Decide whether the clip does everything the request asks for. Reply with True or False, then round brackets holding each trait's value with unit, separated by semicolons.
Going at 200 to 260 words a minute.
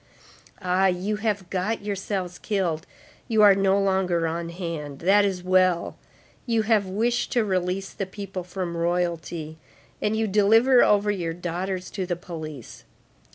False (150 wpm)